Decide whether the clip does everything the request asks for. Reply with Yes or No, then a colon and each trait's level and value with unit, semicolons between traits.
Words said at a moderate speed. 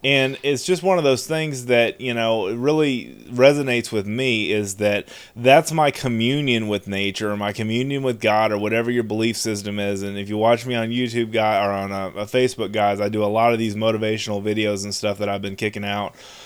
No: fast, 220 wpm